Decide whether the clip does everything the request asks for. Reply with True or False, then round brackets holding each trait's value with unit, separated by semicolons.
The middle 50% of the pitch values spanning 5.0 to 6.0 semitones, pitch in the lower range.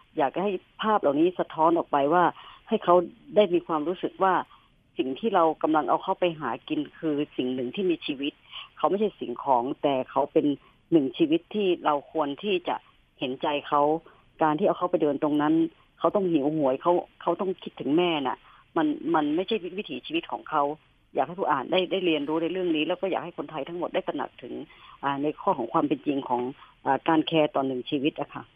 False (5.3 semitones; 165 Hz)